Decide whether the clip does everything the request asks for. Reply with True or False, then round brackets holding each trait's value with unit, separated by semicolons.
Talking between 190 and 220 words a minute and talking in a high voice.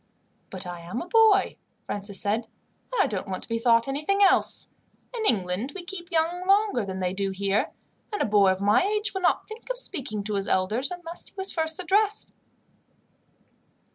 True (195 wpm; 260 Hz)